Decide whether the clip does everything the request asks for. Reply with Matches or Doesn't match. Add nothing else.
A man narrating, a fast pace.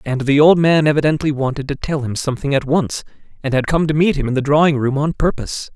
Matches